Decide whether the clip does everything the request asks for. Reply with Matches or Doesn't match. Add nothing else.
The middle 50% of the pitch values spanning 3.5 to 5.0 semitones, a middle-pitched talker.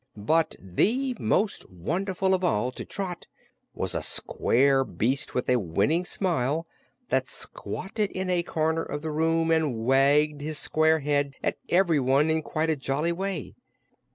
Matches